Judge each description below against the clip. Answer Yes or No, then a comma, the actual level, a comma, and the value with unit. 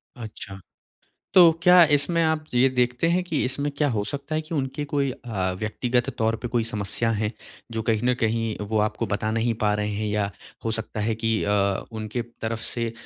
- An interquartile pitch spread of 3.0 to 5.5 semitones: Yes, average, 3.9 semitones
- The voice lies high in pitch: No, low, 115 Hz